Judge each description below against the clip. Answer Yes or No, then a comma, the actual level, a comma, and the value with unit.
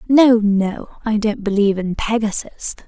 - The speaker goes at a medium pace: Yes, average, 145 wpm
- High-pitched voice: Yes, high, 215 Hz